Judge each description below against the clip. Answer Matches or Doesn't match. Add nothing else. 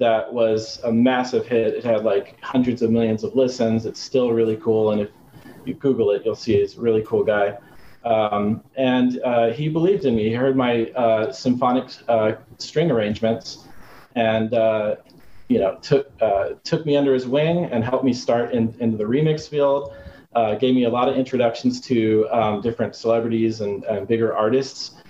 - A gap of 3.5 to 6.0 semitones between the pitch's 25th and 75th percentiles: Doesn't match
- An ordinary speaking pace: Matches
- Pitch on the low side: Matches